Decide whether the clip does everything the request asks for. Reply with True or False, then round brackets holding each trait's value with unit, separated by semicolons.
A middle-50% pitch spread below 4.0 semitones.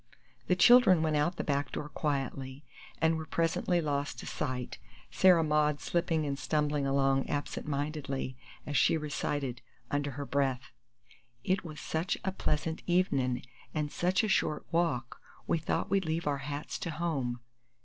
True (3.0 semitones)